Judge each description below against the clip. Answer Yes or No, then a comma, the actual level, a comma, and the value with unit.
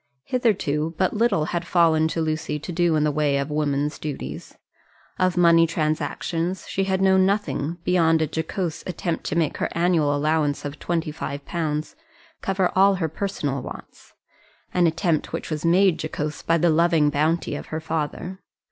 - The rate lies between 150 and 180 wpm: Yes, average, 170 wpm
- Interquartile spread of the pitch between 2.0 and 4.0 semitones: Yes, average, 2.7 semitones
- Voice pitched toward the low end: No, medium, 165 Hz